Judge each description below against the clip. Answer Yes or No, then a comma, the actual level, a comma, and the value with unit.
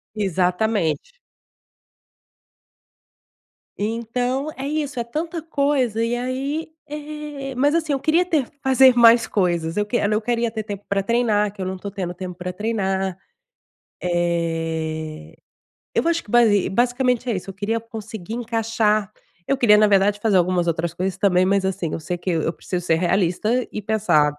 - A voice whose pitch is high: Yes, high, 210 Hz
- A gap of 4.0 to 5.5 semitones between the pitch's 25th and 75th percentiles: Yes, average, 5.2 semitones